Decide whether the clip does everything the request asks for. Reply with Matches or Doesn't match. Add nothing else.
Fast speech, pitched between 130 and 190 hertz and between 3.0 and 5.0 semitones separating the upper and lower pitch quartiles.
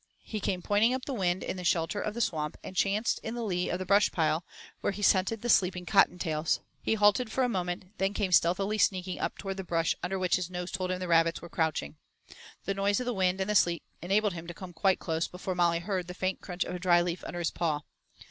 Doesn't match